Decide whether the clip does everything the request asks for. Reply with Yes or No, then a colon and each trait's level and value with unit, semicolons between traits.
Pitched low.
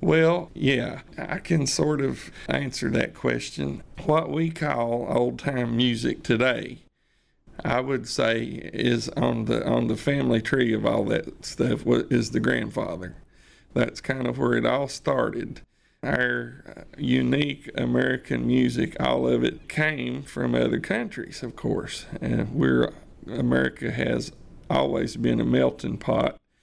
Yes: low, 120 Hz